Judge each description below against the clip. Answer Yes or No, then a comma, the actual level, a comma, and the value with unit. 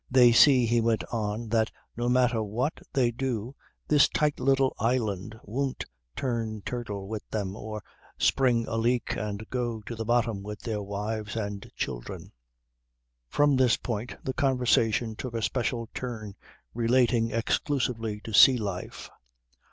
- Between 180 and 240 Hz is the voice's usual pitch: No, low, 115 Hz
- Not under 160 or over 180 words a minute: No, average, 145 wpm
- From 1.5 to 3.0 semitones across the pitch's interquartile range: Yes, average, 2.7 semitones